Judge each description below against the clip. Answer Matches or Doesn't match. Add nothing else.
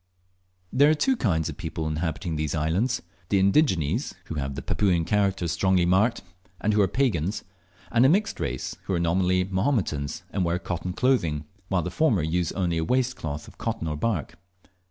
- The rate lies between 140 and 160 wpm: Doesn't match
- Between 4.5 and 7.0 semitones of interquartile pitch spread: Matches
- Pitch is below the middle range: Matches